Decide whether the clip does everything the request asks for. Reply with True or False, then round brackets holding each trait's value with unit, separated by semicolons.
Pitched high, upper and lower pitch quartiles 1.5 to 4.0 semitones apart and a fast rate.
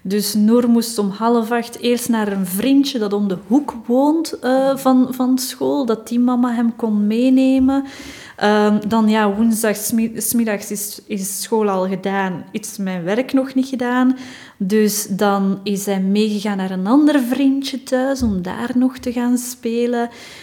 False (230 Hz; 3.6 semitones; 165 wpm)